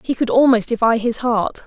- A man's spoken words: No, female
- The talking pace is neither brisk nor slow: No, fast, 215 wpm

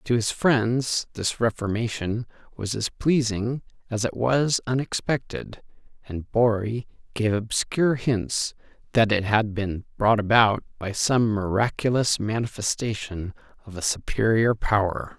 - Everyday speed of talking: No, slow, 120 wpm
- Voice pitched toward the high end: No, low, 110 Hz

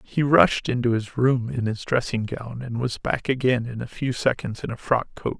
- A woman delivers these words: No, male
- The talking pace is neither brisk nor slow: No, fast, 235 wpm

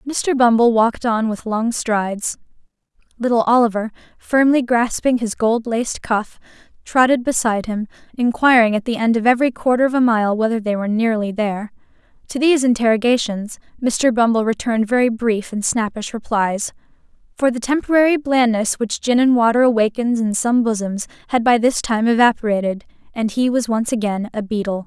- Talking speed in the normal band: Yes, average, 165 wpm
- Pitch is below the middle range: No, high, 230 Hz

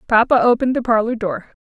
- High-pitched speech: Yes, high, 225 Hz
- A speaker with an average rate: Yes, average, 185 wpm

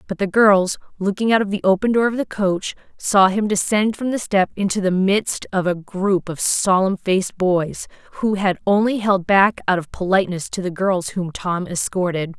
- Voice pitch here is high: Yes, high, 195 Hz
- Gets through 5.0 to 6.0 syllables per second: No, 4.8 syllables/s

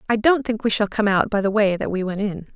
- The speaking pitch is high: Yes, high, 210 Hz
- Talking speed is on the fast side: Yes, fast, 330 wpm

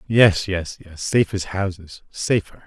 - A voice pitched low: Yes, very low, 95 Hz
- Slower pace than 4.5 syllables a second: Yes, 4.2 syllables/s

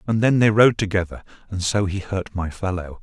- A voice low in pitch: Yes, low, 100 Hz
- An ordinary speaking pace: No, fast, 220 wpm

